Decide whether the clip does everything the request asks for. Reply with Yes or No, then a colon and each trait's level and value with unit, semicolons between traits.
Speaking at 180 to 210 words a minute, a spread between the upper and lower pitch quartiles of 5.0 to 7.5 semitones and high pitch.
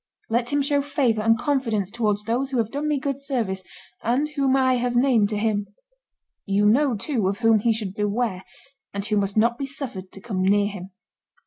No: fast, 205 wpm; average, 4.5 semitones; high, 225 Hz